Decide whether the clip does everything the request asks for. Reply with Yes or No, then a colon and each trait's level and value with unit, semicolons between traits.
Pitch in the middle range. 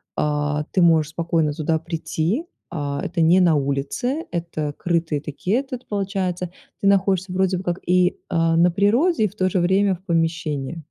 Yes: medium, 175 Hz